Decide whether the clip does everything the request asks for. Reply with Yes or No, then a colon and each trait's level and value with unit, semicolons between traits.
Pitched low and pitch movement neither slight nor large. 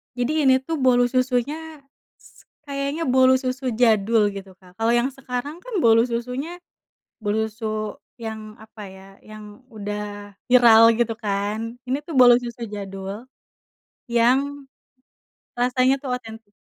No: high, 235 Hz; average, 3.2 semitones